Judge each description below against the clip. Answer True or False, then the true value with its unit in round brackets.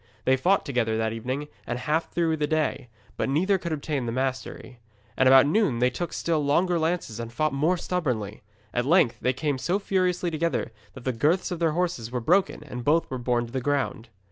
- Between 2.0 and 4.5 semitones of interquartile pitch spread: False (5.2 semitones)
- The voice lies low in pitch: False (145 Hz)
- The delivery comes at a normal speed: False (215 wpm)